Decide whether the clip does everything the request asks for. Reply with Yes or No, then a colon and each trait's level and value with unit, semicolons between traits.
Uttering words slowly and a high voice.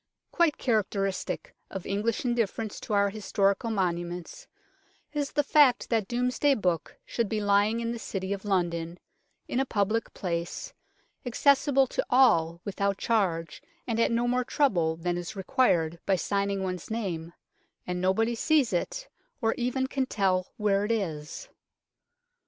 No: average, 145 wpm; high, 205 Hz